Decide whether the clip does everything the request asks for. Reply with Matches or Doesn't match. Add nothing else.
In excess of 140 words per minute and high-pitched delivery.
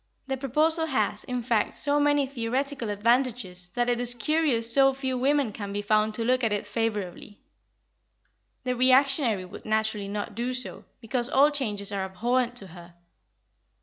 Matches